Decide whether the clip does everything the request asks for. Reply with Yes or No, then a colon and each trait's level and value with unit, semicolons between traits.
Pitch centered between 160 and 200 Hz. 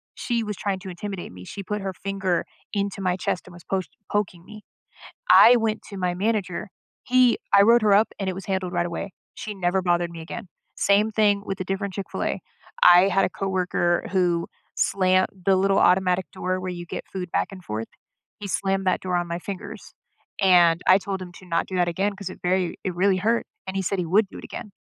Yes: high, 190 Hz